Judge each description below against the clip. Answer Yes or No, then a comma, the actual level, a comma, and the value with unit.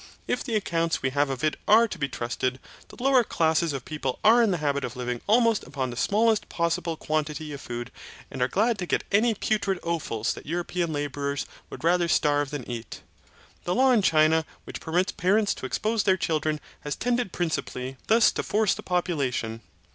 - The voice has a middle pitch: Yes, medium, 160 Hz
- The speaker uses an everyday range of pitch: No, wide, 6.5 semitones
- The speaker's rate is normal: Yes, average, 195 wpm